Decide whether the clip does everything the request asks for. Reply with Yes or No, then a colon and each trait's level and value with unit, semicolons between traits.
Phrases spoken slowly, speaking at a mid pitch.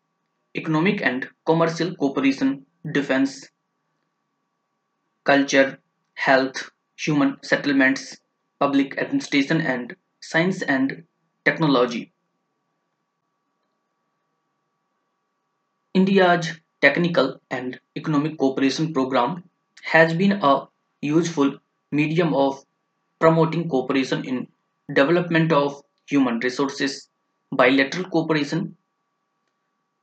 Yes: slow, 70 wpm; medium, 160 Hz